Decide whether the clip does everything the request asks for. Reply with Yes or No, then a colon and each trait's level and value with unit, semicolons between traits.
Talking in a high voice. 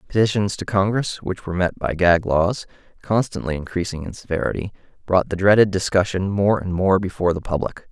No: very low, 95 Hz